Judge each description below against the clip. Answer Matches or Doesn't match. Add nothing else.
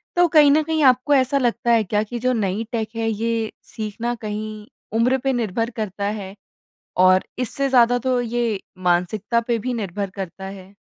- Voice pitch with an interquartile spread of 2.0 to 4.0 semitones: Matches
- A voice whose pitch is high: Matches